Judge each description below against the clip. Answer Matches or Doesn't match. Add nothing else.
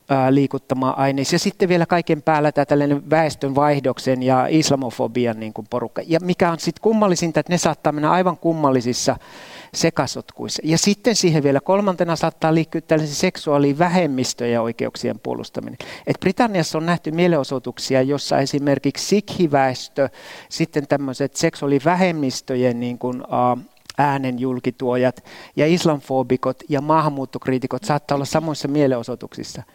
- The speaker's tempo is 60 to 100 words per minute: Doesn't match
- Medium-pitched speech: Matches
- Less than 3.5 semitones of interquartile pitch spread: Doesn't match